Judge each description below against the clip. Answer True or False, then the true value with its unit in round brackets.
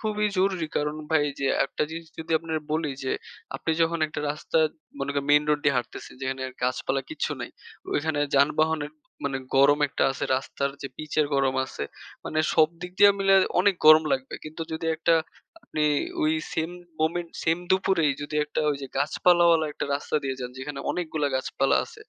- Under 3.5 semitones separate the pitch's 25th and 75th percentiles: True (2.9 semitones)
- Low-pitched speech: False (155 Hz)